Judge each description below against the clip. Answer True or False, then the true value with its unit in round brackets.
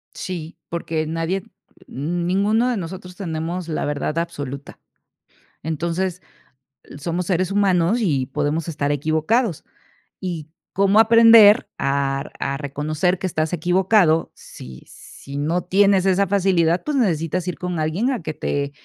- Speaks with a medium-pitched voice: True (170 Hz)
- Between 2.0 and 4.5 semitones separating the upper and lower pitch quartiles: True (3.6 semitones)